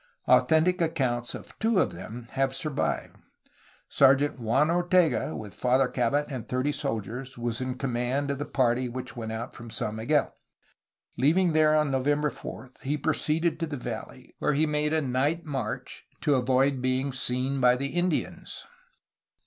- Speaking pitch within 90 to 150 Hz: Yes, low, 135 Hz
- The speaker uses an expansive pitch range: No, average, 3.4 semitones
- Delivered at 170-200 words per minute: No, average, 160 wpm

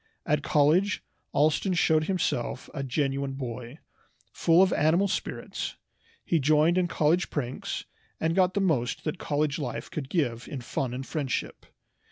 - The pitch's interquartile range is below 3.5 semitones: No, average, 4.1 semitones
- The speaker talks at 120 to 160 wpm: Yes, average, 150 wpm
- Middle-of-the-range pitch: Yes, medium, 150 Hz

